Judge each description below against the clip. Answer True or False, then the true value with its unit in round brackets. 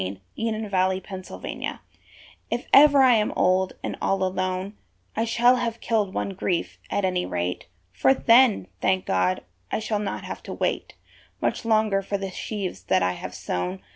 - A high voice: True (195 Hz)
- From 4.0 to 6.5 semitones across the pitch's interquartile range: False (3.5 semitones)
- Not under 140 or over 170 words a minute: False (185 wpm)